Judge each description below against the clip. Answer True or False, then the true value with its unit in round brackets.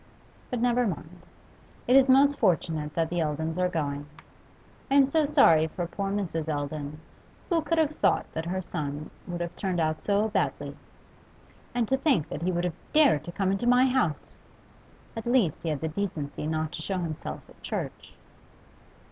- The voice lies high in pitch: False (175 Hz)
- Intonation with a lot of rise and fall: True (7.5 semitones)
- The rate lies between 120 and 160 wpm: False (180 wpm)